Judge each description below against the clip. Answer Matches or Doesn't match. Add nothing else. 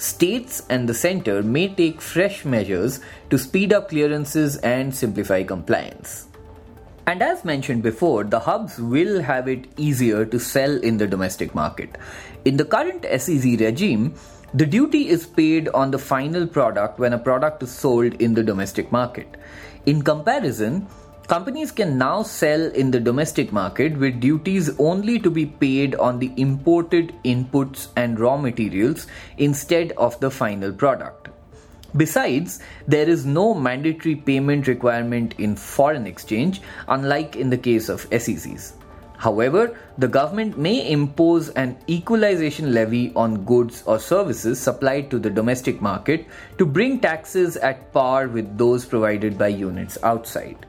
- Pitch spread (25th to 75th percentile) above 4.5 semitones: Matches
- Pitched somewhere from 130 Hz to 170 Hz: Matches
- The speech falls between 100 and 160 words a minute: Matches